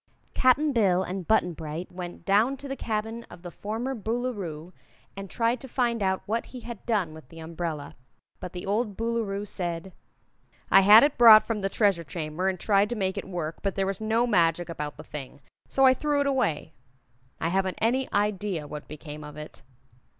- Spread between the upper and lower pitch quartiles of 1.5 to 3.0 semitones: No, average, 5.3 semitones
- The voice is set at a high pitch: Yes, high, 195 Hz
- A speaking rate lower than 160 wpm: No, average, 195 wpm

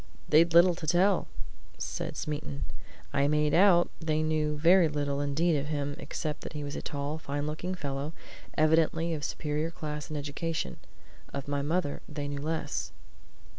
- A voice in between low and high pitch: Yes, medium, 150 Hz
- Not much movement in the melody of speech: Yes, narrow, 2.3 semitones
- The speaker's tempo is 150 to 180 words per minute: Yes, average, 170 wpm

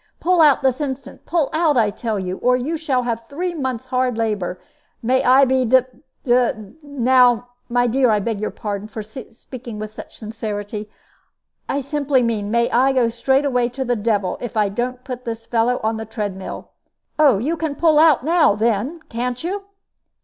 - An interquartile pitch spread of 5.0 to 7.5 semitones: No, average, 3.5 semitones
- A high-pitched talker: Yes, high, 245 Hz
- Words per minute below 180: No, average, 185 wpm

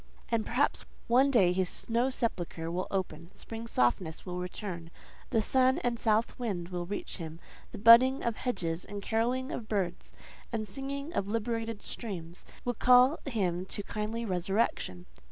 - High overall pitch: Yes, high, 215 Hz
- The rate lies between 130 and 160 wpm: Yes, average, 155 wpm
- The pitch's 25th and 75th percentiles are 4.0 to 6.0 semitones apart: Yes, average, 4.8 semitones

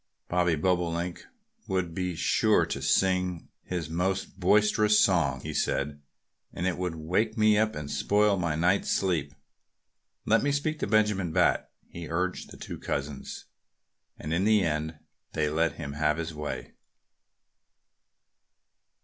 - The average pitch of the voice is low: Yes, very low, 90 Hz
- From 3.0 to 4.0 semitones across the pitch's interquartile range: Yes, average, 3.6 semitones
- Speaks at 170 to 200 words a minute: No, average, 145 wpm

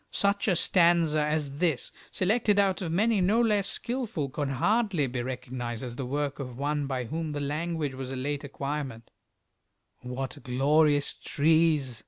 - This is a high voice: No, medium, 145 Hz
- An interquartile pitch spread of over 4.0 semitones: Yes, average, 4.5 semitones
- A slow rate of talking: No, average, 160 wpm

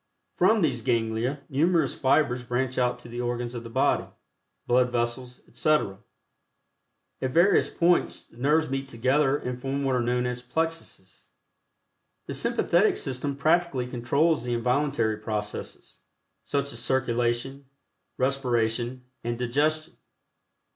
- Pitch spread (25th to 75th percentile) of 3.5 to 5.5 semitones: No, average, 2.8 semitones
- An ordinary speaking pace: No, slow, 125 wpm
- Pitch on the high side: No, low, 125 Hz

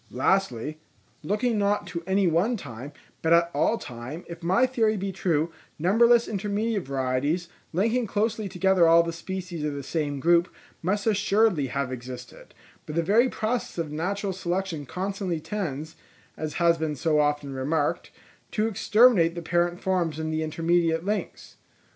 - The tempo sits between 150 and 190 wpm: Yes, average, 155 wpm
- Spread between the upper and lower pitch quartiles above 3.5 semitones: Yes, average, 4.5 semitones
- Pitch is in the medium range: Yes, medium, 175 Hz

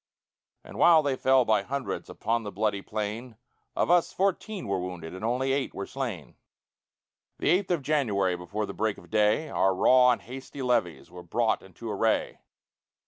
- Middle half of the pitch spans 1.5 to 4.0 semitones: No, wide, 5.5 semitones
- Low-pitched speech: Yes, low, 115 Hz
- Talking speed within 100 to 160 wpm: No, average, 175 wpm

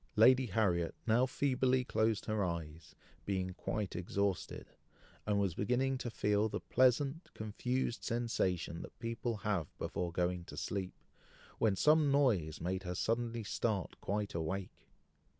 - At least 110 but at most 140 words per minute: Yes, slow, 135 wpm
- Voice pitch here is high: No, low, 105 Hz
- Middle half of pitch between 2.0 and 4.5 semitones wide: No, average, 4.9 semitones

